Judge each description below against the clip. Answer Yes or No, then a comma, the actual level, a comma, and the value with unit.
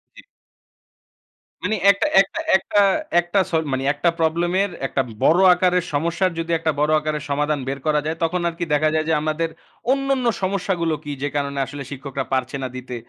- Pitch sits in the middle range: Yes, medium, 160 Hz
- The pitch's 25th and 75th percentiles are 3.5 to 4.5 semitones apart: Yes, average, 3.8 semitones